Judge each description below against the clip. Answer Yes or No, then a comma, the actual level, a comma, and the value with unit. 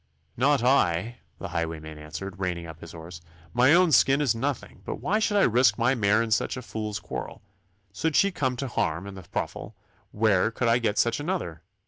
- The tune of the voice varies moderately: No, wide, 6.6 semitones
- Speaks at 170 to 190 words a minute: No, average, 200 wpm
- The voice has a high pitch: No, low, 115 Hz